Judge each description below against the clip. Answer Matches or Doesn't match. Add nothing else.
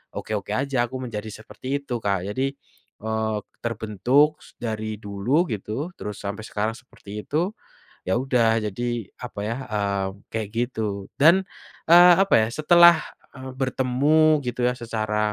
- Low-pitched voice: Matches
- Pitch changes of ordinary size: Matches